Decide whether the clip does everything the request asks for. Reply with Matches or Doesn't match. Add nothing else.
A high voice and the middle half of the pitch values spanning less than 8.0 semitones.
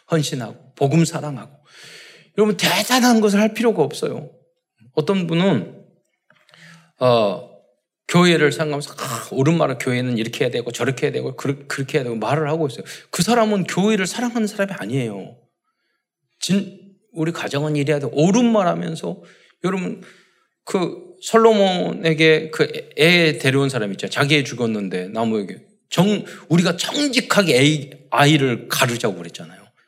Doesn't match